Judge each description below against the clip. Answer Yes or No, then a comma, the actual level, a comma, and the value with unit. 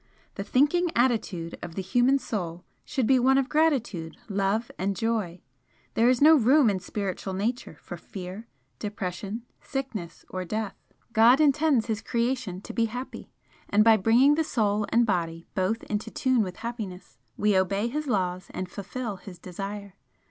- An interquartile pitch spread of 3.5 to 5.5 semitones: Yes, average, 4.8 semitones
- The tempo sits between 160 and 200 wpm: Yes, average, 165 wpm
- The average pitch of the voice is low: No, high, 215 Hz